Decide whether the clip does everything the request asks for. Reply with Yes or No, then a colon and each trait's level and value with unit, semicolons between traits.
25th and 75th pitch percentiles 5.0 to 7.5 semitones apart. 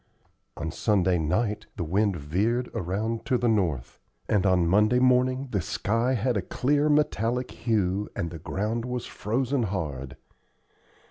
Yes: average, 5.3 semitones